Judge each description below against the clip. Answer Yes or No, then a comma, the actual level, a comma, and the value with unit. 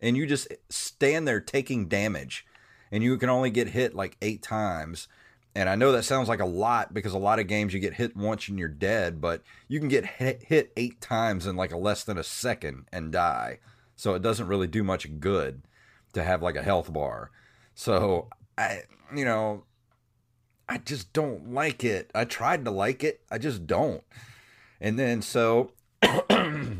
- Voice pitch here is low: Yes, low, 110 Hz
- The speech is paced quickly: No, average, 195 wpm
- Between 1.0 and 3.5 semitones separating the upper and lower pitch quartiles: No, average, 4.2 semitones